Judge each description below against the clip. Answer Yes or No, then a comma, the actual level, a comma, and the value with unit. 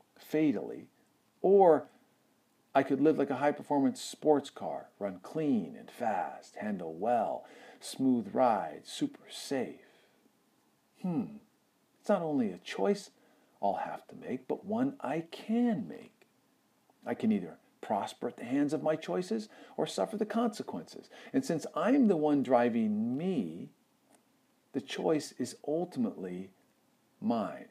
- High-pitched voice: Yes, high, 205 Hz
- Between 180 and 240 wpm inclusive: No, slow, 135 wpm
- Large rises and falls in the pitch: Yes, wide, 7.5 semitones